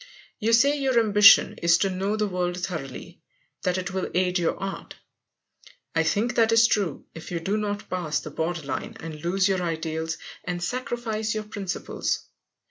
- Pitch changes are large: No, average, 4.0 semitones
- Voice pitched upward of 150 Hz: Yes, medium, 185 Hz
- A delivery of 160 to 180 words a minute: Yes, average, 175 wpm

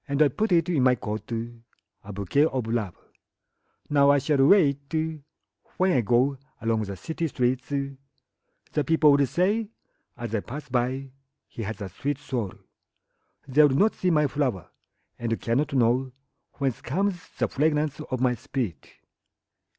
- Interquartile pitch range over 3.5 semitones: Yes, average, 4.1 semitones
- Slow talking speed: Yes, slow, 120 wpm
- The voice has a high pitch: No, low, 135 Hz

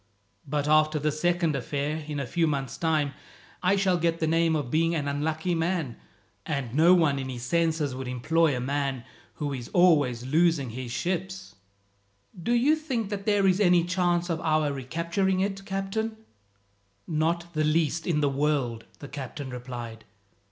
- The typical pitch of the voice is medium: Yes, medium, 155 Hz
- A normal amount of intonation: Yes, average, 4.0 semitones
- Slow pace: No, average, 170 wpm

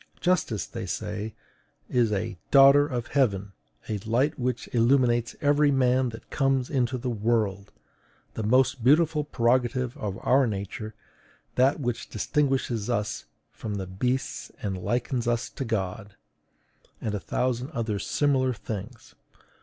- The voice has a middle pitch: No, low, 120 Hz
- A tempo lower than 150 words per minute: Yes, slow, 135 wpm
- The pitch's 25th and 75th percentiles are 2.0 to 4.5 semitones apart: Yes, average, 3.6 semitones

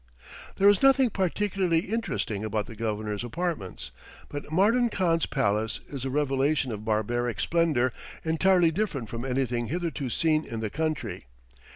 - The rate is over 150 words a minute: No, average, 145 wpm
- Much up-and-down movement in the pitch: Yes, wide, 7.3 semitones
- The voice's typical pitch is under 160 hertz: Yes, medium, 140 Hz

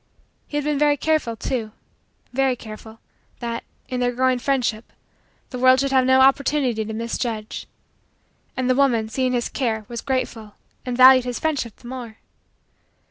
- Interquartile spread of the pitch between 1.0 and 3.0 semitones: Yes, narrow, 2.4 semitones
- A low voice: No, very high, 250 Hz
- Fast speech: No, average, 160 wpm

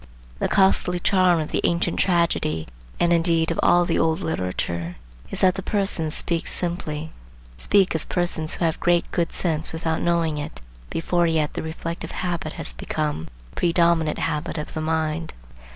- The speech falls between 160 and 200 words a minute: Yes, average, 165 wpm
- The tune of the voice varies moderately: No, narrow, 2.2 semitones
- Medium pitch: Yes, medium, 165 Hz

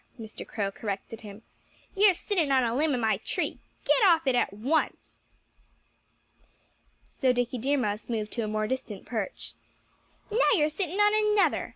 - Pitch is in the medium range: No, very high, 250 Hz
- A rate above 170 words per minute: No, average, 165 wpm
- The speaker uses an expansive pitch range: Yes, wide, 7.0 semitones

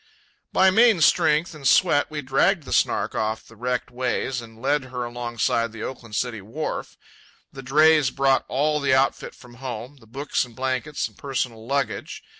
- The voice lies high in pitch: No, low, 130 Hz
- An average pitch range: Yes, average, 3.5 semitones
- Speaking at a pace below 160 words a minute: No, average, 180 wpm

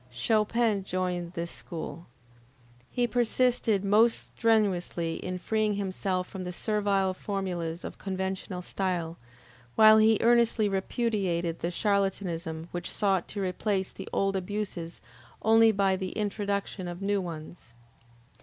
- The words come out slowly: Yes, slow, 125 wpm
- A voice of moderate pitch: No, high, 195 Hz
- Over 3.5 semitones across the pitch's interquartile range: No, average, 3.0 semitones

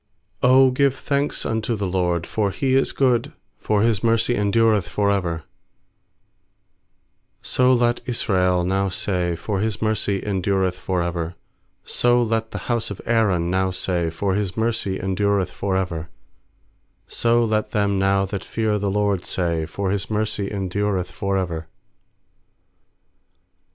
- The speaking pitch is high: No, low, 100 Hz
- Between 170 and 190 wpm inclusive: No, average, 150 wpm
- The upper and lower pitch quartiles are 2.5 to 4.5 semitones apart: Yes, average, 3.4 semitones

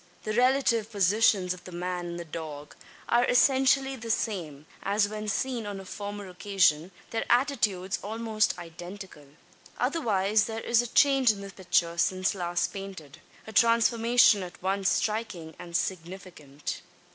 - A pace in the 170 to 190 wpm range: No, average, 145 wpm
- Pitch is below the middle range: No, high, 200 Hz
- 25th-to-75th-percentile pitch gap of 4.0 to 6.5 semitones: Yes, average, 4.3 semitones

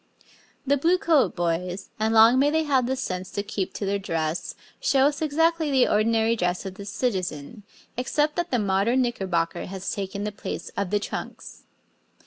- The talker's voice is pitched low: No, high, 220 Hz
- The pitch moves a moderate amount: No, wide, 5.9 semitones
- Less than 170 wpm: No, average, 175 wpm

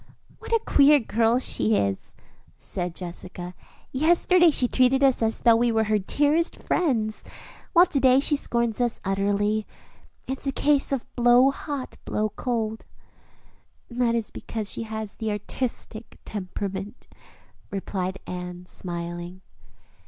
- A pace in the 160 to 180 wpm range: No, slow, 135 wpm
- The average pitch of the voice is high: Yes, high, 225 Hz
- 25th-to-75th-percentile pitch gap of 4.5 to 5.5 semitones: Yes, average, 4.8 semitones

